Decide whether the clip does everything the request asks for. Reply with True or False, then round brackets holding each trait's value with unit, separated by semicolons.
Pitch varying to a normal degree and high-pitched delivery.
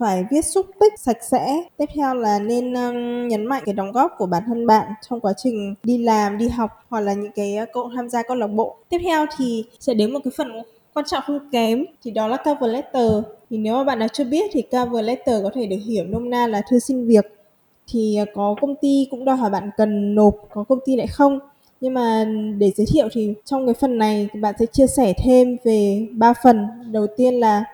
True (3.5 semitones; 235 Hz)